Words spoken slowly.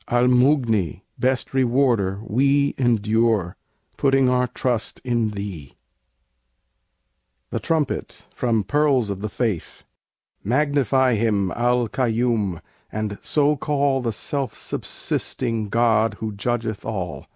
Yes: slow, 110 wpm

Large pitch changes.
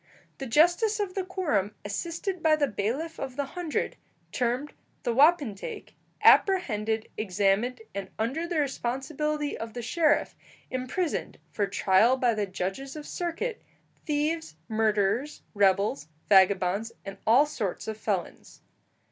Yes: wide, 7.0 semitones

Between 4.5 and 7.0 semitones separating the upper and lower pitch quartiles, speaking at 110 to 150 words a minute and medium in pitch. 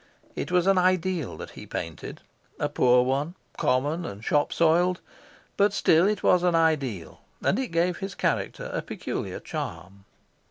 No: wide, 5.5 semitones; average, 160 wpm; medium, 165 Hz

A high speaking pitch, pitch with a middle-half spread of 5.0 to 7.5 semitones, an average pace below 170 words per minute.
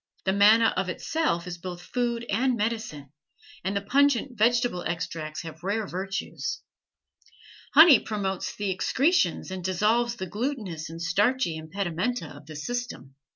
Yes: high, 200 Hz; wide, 5.6 semitones; average, 140 wpm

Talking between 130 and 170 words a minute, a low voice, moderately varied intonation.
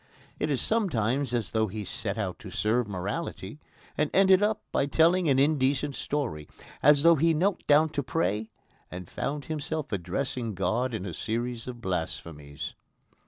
No: average, 160 wpm; low, 130 Hz; wide, 6.1 semitones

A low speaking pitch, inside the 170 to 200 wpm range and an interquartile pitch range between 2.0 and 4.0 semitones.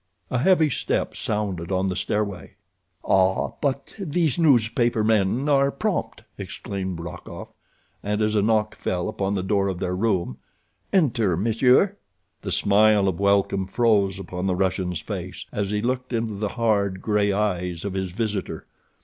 No: low, 105 Hz; average, 155 wpm; average, 3.4 semitones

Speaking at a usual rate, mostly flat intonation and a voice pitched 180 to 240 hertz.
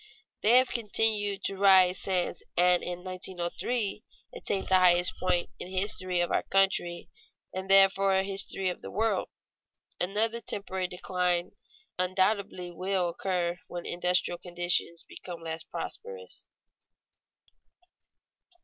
No: slow, 125 wpm; narrow, 1.9 semitones; medium, 185 Hz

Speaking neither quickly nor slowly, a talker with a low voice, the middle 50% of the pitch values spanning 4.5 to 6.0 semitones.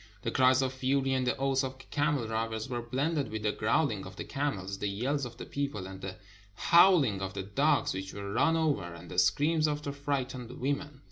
No: fast, 225 wpm; low, 130 Hz; wide, 5.5 semitones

